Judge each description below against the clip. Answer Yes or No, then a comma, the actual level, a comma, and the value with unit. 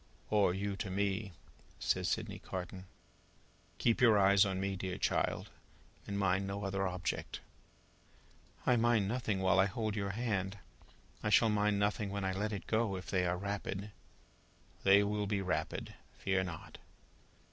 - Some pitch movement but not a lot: No, narrow, 1.6 semitones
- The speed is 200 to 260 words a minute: No, average, 160 wpm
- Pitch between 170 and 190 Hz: No, low, 100 Hz